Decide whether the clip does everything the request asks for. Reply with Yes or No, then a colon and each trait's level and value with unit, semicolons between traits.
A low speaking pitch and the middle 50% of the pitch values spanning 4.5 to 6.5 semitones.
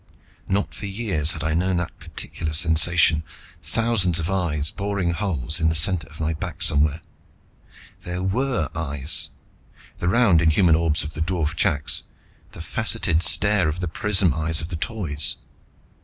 No: very low, 85 Hz; average, 3.4 semitones